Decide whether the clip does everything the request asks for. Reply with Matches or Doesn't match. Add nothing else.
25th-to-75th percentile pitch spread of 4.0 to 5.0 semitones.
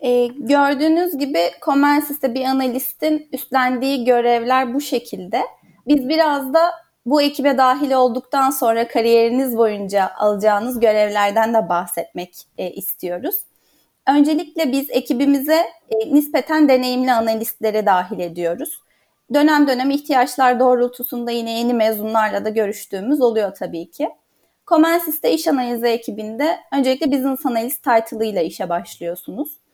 Matches